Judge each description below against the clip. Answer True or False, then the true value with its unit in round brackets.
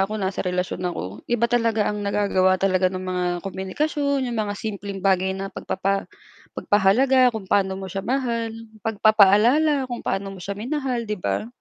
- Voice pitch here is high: True (205 Hz)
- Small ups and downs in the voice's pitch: False (3.7 semitones)